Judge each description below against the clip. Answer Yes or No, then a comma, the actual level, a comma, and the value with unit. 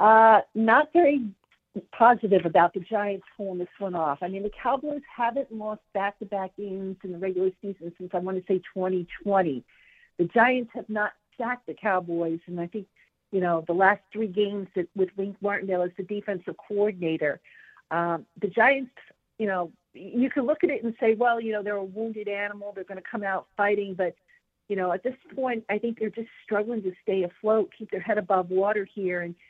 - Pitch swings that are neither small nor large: Yes, average, 3.0 semitones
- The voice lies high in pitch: Yes, high, 205 Hz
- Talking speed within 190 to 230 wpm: Yes, average, 200 wpm